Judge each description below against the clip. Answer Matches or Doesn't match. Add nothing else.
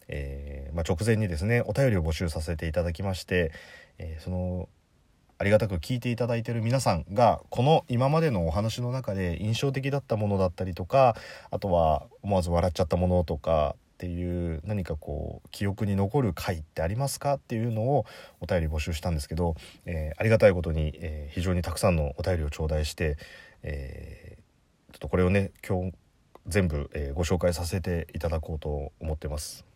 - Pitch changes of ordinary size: Matches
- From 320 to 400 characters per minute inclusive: Matches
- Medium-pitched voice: Doesn't match